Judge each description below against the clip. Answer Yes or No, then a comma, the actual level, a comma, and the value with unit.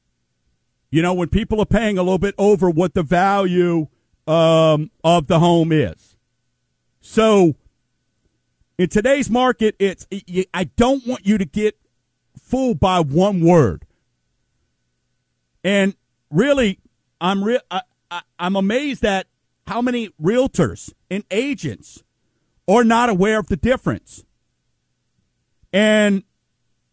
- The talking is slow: Yes, slow, 115 wpm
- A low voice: No, medium, 185 Hz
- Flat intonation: No, average, 5.3 semitones